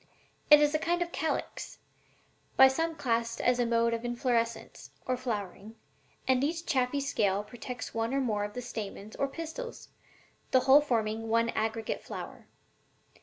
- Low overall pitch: No, high, 245 Hz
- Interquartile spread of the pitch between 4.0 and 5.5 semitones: No, average, 3.6 semitones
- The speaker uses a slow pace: No, average, 160 wpm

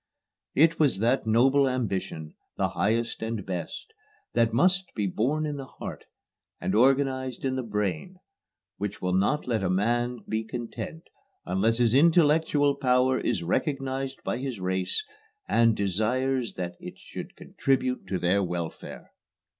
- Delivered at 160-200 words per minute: No, average, 145 wpm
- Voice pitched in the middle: No, low, 120 Hz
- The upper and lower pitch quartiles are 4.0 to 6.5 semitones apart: Yes, average, 5.0 semitones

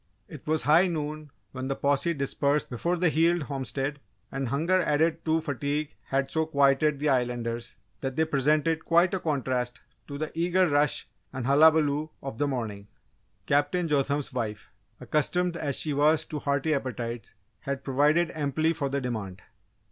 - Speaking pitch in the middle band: Yes, medium, 145 Hz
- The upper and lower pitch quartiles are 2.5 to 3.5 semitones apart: Yes, average, 2.9 semitones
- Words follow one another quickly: No, average, 160 wpm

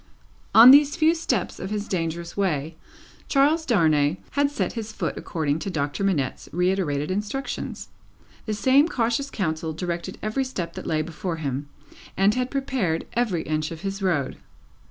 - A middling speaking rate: Yes, average, 155 wpm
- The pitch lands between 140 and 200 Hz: Yes, high, 190 Hz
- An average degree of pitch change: No, wide, 7.5 semitones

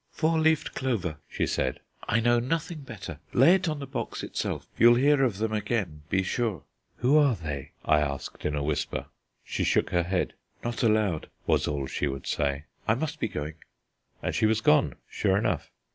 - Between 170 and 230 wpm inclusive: Yes, average, 190 wpm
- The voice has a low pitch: Yes, low, 110 Hz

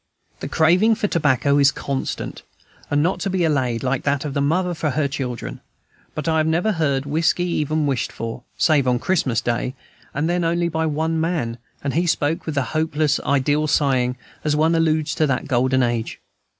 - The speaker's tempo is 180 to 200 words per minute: Yes, average, 190 wpm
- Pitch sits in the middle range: Yes, medium, 150 Hz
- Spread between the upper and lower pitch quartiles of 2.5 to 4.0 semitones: Yes, average, 3.4 semitones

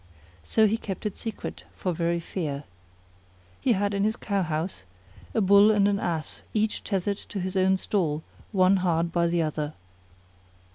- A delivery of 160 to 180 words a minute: Yes, average, 170 wpm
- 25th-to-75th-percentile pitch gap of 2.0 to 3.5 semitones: Yes, average, 3.2 semitones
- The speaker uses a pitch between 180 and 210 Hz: Yes, high, 190 Hz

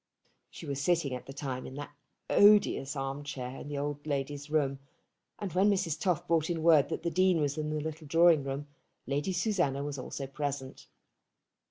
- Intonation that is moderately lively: Yes, average, 3.3 semitones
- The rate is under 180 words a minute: No, average, 190 wpm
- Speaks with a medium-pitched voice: Yes, medium, 145 Hz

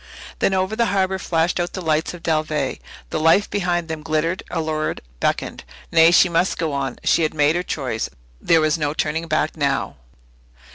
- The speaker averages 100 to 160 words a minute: No, average, 185 wpm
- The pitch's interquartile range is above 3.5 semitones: No, narrow, 2.4 semitones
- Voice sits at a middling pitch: Yes, medium, 160 Hz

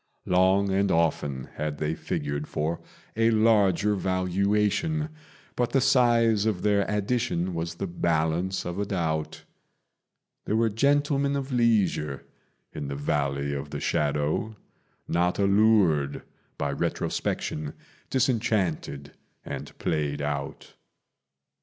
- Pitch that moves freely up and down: Yes, wide, 6.4 semitones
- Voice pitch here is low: Yes, very low, 95 Hz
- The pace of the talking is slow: Yes, slow, 115 wpm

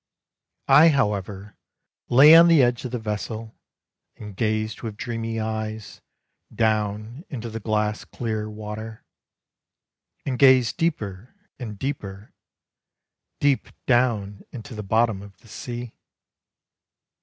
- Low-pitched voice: Yes, low, 110 Hz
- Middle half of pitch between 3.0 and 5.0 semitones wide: No, narrow, 2.5 semitones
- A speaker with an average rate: No, slow, 115 wpm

